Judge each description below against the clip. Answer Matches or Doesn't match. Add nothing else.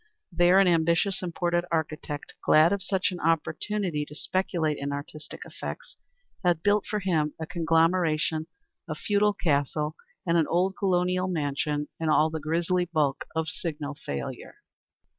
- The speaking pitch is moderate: Matches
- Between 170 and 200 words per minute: Doesn't match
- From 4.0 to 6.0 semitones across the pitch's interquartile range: Doesn't match